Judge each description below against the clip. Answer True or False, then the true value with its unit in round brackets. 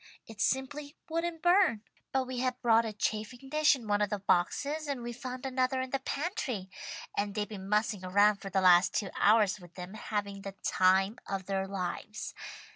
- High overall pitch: True (215 Hz)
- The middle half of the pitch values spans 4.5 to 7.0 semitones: True (4.8 semitones)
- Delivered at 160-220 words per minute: True (195 wpm)